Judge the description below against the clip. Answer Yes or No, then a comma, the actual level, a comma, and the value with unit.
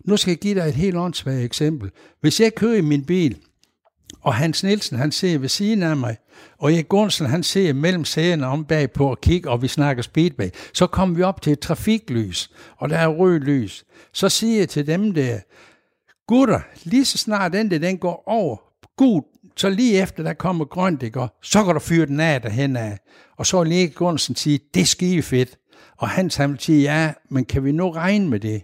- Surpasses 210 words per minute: Yes, average, 220 wpm